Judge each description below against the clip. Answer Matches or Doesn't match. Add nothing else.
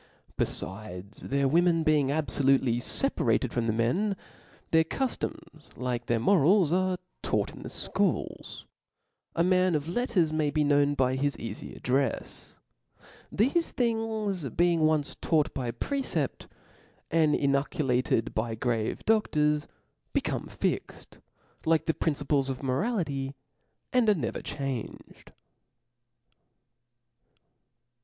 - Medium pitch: Matches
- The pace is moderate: Doesn't match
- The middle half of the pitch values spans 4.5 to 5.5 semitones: Matches